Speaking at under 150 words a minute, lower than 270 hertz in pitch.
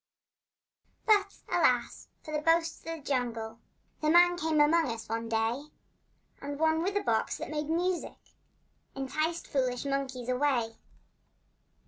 No: slow, 135 wpm; very high, 290 Hz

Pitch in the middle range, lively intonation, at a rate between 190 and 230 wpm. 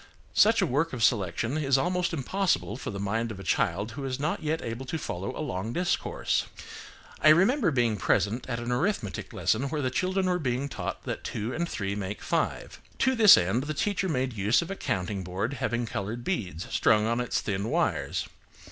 No: low, 125 Hz; wide, 7.0 semitones; average, 200 wpm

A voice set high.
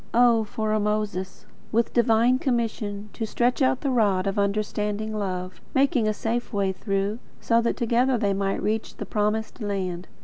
Yes: high, 215 Hz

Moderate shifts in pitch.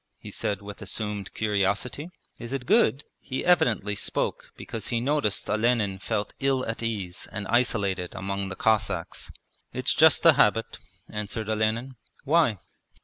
Yes: average, 4.2 semitones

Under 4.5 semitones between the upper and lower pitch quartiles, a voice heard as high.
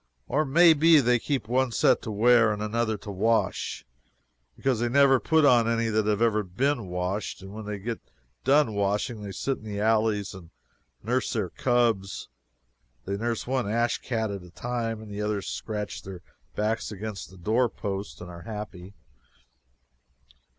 No: average, 3.0 semitones; low, 110 Hz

